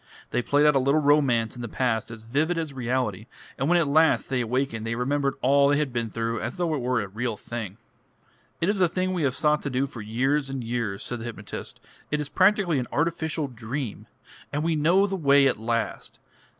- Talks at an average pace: No, fast, 225 wpm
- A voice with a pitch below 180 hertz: Yes, low, 135 Hz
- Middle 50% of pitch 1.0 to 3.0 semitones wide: No, average, 4.3 semitones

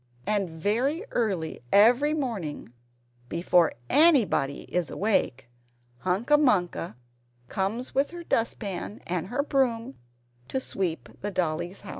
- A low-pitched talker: No, high, 205 Hz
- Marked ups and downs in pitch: Yes, wide, 6.7 semitones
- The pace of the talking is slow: Yes, slow, 120 wpm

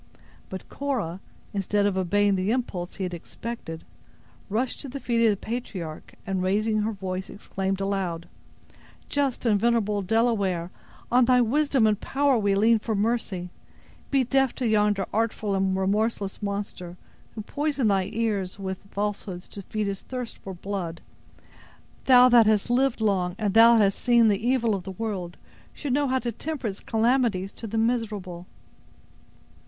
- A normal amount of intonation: Yes, average, 3.6 semitones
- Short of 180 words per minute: Yes, average, 160 wpm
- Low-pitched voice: No, high, 210 Hz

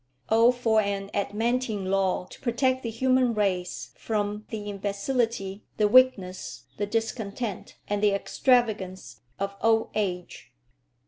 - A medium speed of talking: No, slow, 125 wpm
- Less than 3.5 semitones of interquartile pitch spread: Yes, average, 2.9 semitones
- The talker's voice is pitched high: Yes, high, 210 Hz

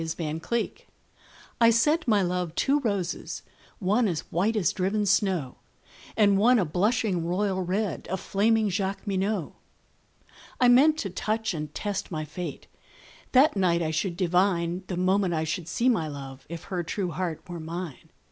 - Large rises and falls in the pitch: No, average, 4.0 semitones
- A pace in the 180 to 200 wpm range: No, average, 165 wpm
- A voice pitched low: No, high, 190 Hz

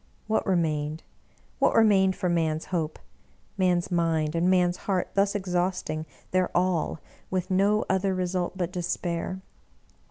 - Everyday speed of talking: Yes, average, 145 wpm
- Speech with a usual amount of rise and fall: No, narrow, 2.0 semitones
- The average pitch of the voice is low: No, medium, 180 Hz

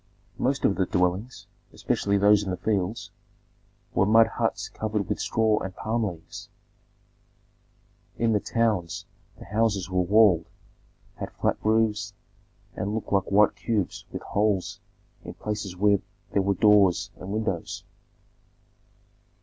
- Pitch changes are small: Yes, narrow, 2.2 semitones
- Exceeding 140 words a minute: No, slow, 135 wpm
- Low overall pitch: Yes, low, 105 Hz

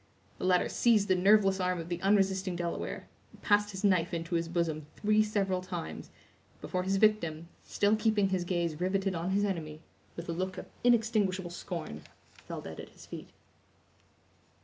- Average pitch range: Yes, average, 3.0 semitones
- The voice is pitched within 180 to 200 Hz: Yes, medium, 185 Hz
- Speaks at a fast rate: No, average, 170 wpm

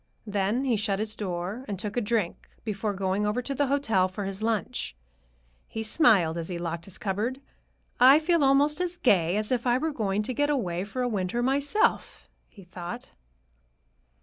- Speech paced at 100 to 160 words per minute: No, average, 185 wpm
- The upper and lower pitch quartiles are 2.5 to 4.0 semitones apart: No, average, 5.2 semitones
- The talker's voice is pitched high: Yes, high, 215 Hz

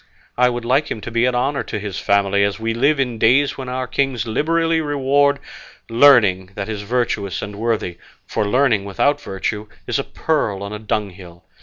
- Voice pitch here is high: No, low, 115 Hz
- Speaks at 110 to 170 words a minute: No, average, 190 wpm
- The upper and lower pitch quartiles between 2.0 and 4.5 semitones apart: No, average, 5.0 semitones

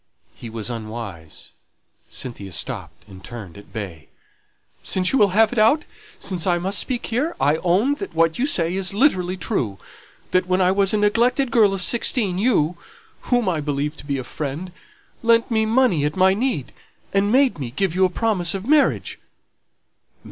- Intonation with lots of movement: Yes, wide, 7.4 semitones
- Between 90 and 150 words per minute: No, average, 180 wpm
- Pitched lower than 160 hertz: No, medium, 185 Hz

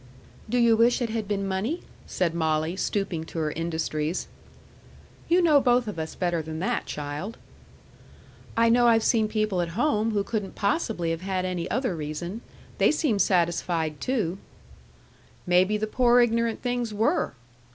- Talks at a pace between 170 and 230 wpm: No, average, 160 wpm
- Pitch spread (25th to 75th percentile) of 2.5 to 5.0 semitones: No, wide, 5.4 semitones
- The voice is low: No, high, 200 Hz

